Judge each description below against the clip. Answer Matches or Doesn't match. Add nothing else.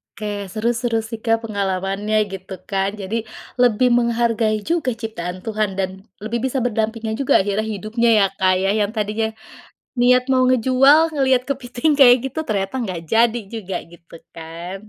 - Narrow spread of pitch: Doesn't match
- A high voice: Matches